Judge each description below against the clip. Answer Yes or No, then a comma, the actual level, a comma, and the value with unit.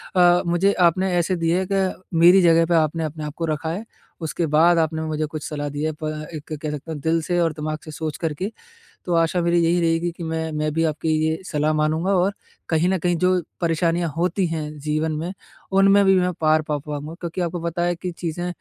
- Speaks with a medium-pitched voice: Yes, medium, 165 Hz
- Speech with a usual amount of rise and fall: No, narrow, 2.2 semitones